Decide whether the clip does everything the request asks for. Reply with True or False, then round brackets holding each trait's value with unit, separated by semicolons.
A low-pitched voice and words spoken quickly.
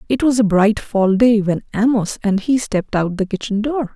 False (215 Hz; 230 wpm)